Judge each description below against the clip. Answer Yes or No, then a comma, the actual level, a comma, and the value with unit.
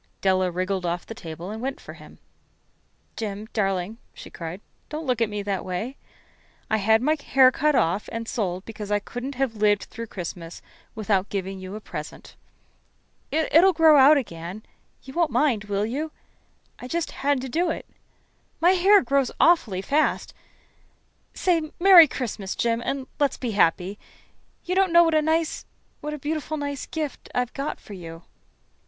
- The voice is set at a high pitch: Yes, high, 230 Hz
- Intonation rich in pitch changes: Yes, wide, 7.4 semitones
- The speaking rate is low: No, average, 170 wpm